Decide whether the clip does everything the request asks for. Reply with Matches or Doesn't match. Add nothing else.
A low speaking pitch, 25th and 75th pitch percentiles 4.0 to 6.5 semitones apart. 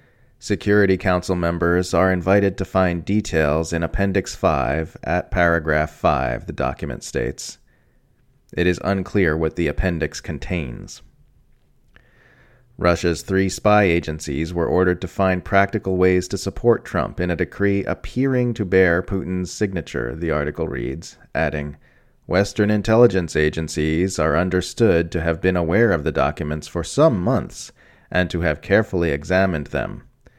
Doesn't match